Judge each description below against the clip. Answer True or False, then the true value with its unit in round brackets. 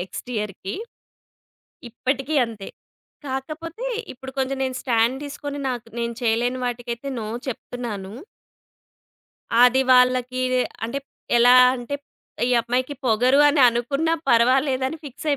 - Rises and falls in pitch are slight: True (2.3 semitones)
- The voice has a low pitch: False (255 Hz)